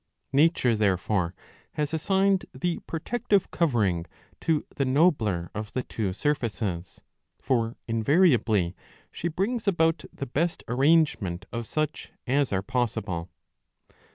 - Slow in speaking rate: Yes, slow, 125 wpm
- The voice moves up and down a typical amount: No, wide, 7.6 semitones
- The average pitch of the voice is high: No, low, 130 Hz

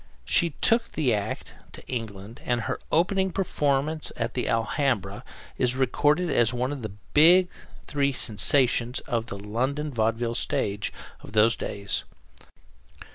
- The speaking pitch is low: Yes, low, 125 Hz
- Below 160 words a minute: Yes, slow, 135 wpm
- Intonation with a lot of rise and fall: No, average, 4.7 semitones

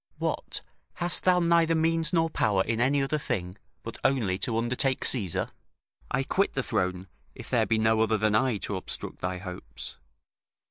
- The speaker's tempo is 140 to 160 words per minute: No, average, 175 wpm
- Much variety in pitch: Yes, wide, 7.3 semitones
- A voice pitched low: Yes, low, 115 Hz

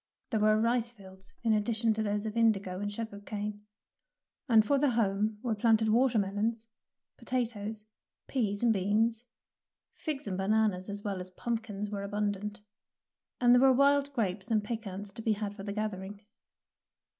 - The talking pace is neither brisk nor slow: Yes, average, 160 wpm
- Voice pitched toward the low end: No, high, 215 Hz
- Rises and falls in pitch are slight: Yes, narrow, 2.1 semitones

